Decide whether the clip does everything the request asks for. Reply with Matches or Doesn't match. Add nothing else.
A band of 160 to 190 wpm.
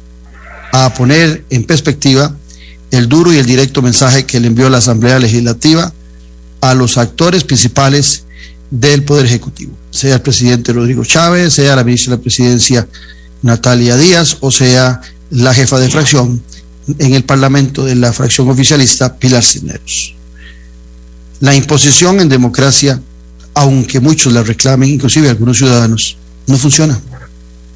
Doesn't match